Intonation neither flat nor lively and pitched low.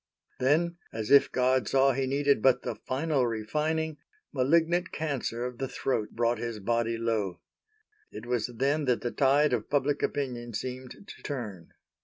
Yes: average, 3.5 semitones; low, 130 Hz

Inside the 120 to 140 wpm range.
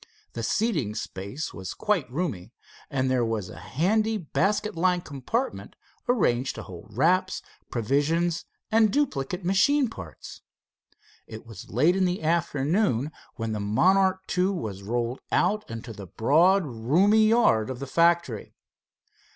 Yes: slow, 135 wpm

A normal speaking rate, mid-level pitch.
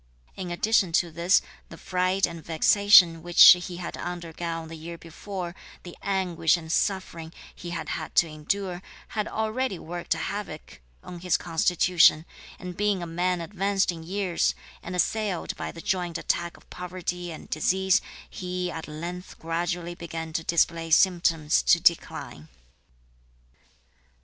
Yes: average, 145 wpm; medium, 175 Hz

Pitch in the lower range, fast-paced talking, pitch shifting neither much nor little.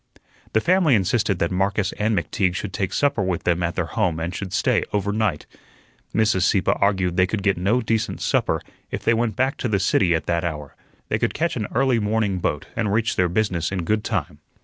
Yes: low, 100 Hz; fast, 220 wpm; average, 3.6 semitones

